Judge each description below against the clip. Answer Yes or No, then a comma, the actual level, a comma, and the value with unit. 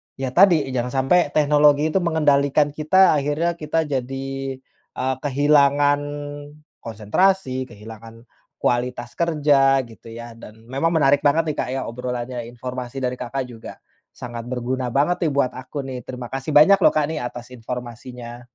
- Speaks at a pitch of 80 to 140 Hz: Yes, low, 135 Hz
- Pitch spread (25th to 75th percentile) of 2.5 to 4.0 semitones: Yes, average, 3.3 semitones